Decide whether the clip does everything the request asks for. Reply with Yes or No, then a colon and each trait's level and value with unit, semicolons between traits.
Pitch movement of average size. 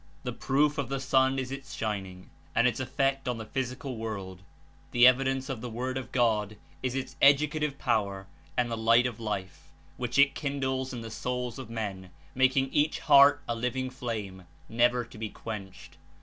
Yes: average, 3.2 semitones